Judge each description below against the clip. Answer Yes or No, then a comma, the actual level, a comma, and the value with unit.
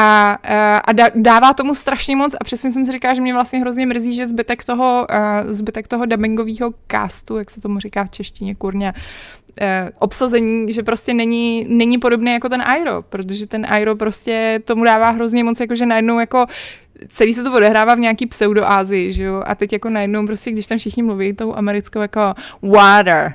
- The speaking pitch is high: Yes, high, 225 Hz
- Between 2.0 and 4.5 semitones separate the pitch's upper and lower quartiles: Yes, narrow, 2.4 semitones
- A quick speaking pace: Yes, fast, 190 wpm